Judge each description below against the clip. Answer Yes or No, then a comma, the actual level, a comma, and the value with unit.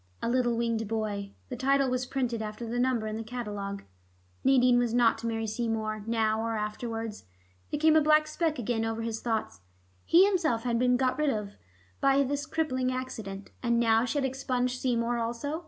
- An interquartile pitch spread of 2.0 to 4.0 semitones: Yes, narrow, 2.6 semitones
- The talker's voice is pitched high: Yes, high, 235 Hz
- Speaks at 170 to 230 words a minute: Yes, average, 190 wpm